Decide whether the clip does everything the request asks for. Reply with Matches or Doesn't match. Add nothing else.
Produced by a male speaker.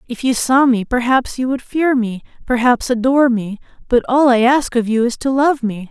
Doesn't match